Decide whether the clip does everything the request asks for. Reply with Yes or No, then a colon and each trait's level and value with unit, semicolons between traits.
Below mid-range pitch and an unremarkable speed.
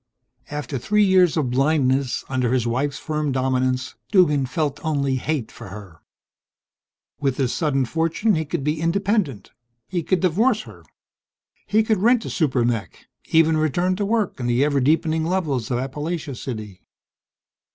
No: medium, 150 Hz; average, 155 wpm